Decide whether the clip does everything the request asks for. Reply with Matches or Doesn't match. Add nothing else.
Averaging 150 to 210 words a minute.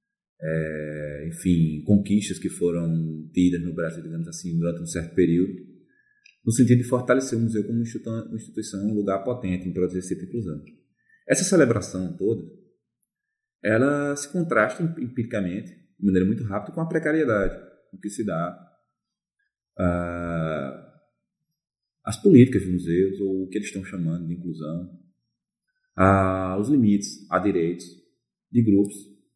Doesn't match